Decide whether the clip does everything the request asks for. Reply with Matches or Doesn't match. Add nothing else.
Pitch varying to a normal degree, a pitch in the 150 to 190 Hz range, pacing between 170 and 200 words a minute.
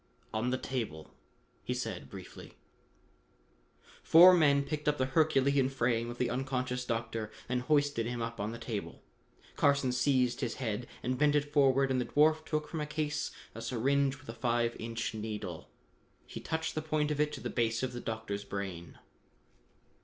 Doesn't match